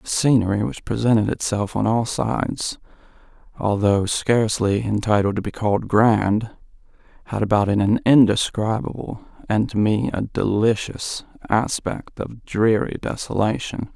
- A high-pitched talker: No, low, 110 Hz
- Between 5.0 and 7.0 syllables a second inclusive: No, 4.5 syllables/s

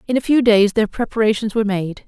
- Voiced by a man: No, female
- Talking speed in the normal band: No, fast, 230 wpm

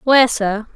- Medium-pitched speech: No, high, 230 Hz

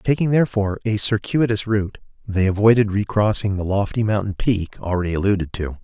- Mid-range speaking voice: No, low, 105 Hz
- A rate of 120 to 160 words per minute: Yes, average, 155 wpm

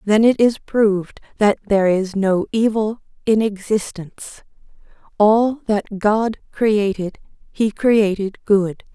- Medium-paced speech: No, slow, 120 wpm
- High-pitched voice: Yes, high, 210 Hz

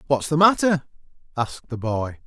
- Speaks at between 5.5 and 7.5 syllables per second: Yes, 5.6 syllables/s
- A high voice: No, medium, 140 Hz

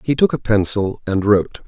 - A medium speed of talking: No, fast, 215 wpm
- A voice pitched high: No, low, 110 Hz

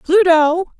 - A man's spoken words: No, female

